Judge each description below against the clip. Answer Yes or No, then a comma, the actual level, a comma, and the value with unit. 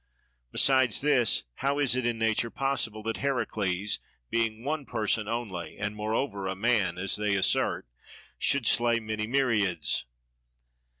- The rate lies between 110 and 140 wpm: Yes, slow, 135 wpm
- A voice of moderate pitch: No, low, 115 Hz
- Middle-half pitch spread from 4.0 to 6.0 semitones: No, average, 3.6 semitones